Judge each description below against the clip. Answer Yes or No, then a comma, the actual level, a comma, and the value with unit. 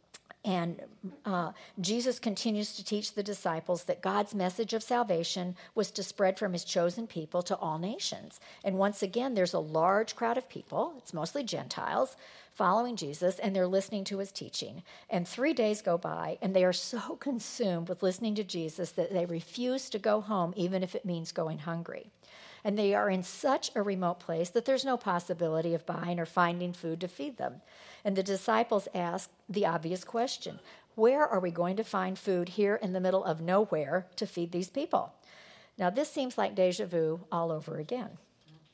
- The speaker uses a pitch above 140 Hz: Yes, high, 190 Hz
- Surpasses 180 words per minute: Yes, average, 190 wpm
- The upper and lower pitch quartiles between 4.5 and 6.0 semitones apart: No, average, 3.9 semitones